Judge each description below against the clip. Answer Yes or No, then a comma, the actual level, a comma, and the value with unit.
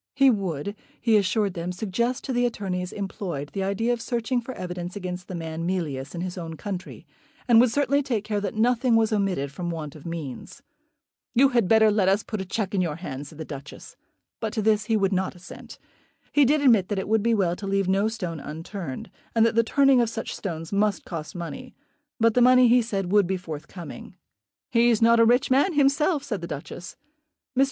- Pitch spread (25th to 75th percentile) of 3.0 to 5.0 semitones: Yes, average, 4.7 semitones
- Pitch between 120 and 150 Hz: No, high, 200 Hz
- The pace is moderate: No, fast, 215 wpm